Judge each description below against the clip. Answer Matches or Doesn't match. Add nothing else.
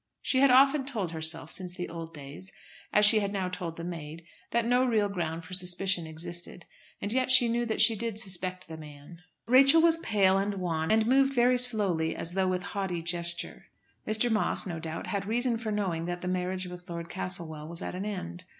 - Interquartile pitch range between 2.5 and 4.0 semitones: Doesn't match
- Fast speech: Matches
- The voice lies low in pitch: Doesn't match